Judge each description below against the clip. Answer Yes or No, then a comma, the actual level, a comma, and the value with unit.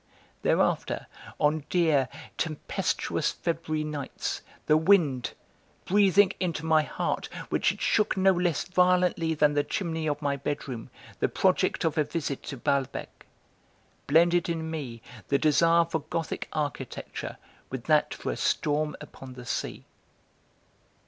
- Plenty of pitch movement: No, average, 2.7 semitones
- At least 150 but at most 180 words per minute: No, slow, 135 wpm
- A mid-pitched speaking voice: Yes, medium, 155 Hz